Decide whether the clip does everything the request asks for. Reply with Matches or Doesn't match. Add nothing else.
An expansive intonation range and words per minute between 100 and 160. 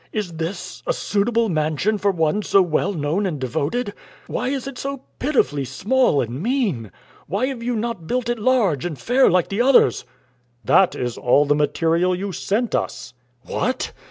Doesn't match